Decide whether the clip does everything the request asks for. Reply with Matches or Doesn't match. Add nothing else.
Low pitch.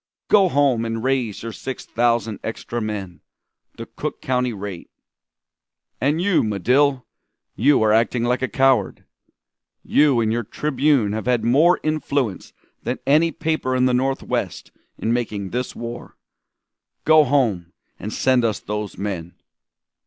Matches